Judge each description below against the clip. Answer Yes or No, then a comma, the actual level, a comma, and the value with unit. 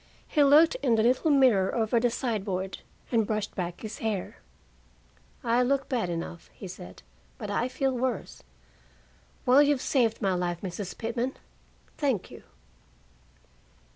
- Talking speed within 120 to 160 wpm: Yes, average, 140 wpm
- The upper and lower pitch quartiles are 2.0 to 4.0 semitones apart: No, average, 5.1 semitones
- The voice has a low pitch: No, high, 230 Hz